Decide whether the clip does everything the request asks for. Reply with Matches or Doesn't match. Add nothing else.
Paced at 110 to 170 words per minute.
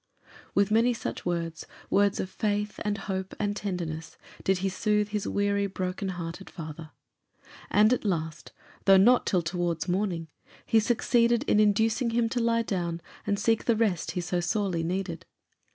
Matches